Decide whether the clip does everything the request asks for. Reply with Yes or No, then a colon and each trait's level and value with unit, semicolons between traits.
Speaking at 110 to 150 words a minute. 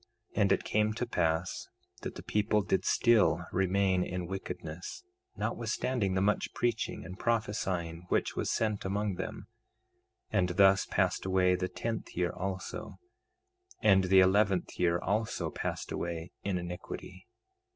Yes: average, 140 wpm